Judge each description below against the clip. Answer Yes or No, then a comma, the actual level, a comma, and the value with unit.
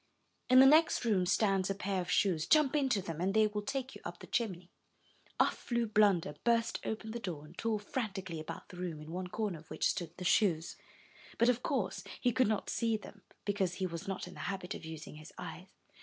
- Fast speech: Yes, fast, 225 wpm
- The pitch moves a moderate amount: Yes, average, 4.2 semitones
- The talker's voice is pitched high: Yes, high, 195 Hz